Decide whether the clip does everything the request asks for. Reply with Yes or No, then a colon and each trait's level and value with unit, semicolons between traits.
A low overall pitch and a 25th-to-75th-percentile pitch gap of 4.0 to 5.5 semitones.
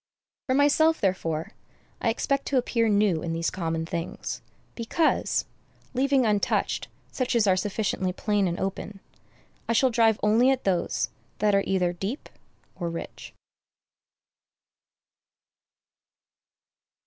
No: high, 210 Hz; average, 5.2 semitones